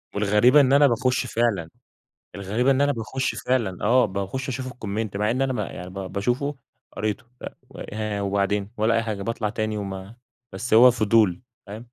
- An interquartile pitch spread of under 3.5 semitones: No, average, 3.8 semitones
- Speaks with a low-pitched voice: Yes, low, 110 Hz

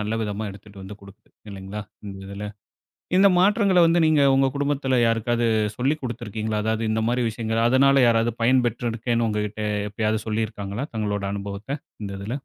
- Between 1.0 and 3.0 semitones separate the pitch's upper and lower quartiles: No, average, 3.7 semitones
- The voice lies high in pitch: No, low, 110 Hz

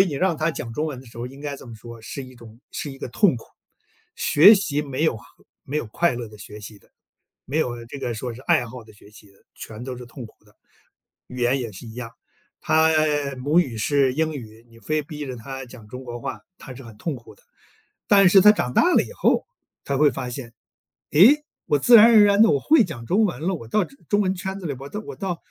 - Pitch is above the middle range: No, low, 135 Hz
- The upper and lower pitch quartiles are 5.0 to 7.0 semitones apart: Yes, wide, 5.6 semitones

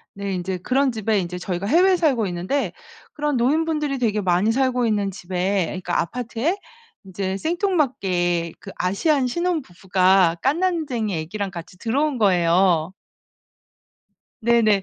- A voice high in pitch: Yes, high, 210 Hz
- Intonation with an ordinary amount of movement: No, wide, 6.9 semitones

